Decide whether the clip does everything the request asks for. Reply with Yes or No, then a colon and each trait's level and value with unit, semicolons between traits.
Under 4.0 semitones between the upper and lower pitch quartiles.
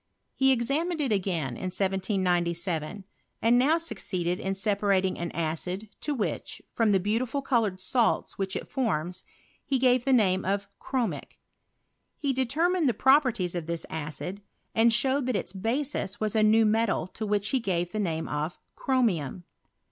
No: wide, 5.5 semitones